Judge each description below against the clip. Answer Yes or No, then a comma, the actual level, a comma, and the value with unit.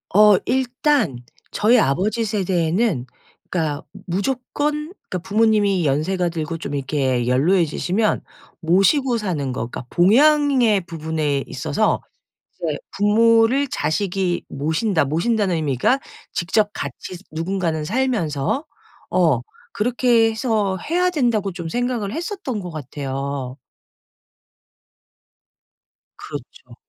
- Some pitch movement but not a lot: No, wide, 6.7 semitones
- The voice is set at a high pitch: Yes, high, 195 Hz